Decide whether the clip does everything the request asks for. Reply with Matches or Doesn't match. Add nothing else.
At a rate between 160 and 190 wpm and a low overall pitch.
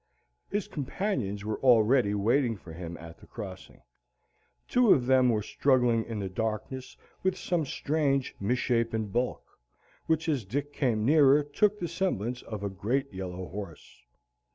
Doesn't match